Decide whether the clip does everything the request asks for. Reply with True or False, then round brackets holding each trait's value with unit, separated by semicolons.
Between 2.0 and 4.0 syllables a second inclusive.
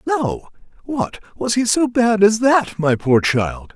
True (3.5 syllables/s)